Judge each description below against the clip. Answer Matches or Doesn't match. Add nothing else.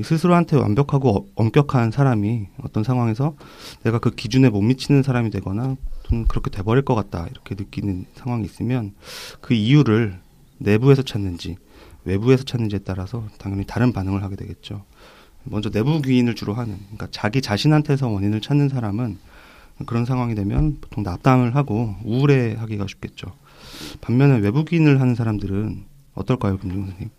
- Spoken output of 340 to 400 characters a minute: Matches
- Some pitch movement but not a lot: Matches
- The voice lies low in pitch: Matches